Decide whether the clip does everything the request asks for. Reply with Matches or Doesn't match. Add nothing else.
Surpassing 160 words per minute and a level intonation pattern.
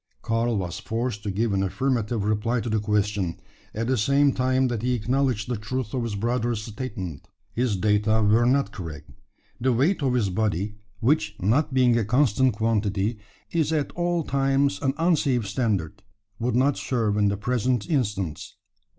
Doesn't match